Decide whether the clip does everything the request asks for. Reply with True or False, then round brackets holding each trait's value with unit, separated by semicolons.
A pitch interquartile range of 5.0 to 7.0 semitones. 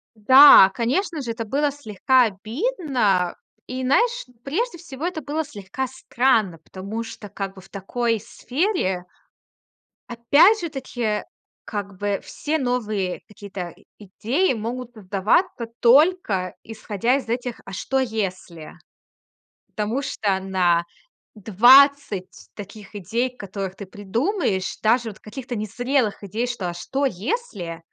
True (5.3 semitones)